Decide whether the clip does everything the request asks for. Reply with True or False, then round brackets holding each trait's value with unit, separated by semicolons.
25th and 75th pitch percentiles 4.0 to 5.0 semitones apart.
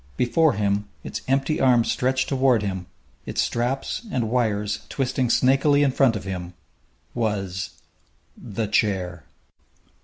True (4.7 semitones)